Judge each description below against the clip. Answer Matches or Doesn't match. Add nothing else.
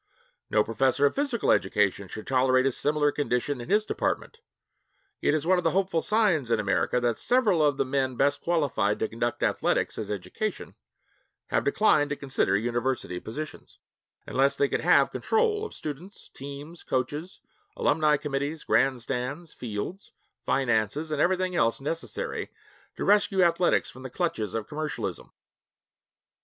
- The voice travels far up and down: Matches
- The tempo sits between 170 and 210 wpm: Doesn't match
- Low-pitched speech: Doesn't match